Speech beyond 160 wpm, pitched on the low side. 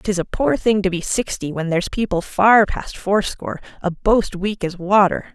No: average, 200 wpm; high, 195 Hz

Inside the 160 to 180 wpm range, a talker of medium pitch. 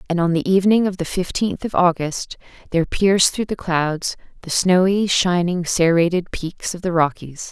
Yes: average, 175 wpm; medium, 175 Hz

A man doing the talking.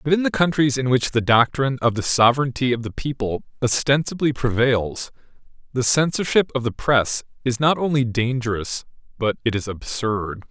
Yes: male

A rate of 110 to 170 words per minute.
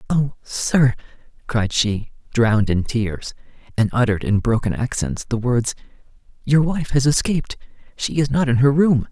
Yes: average, 150 wpm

